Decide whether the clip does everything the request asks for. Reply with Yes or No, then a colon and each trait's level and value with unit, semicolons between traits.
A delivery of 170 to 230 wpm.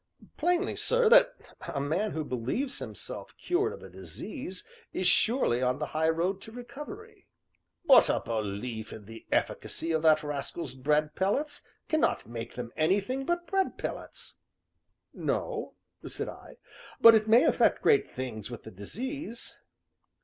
No: average, 150 wpm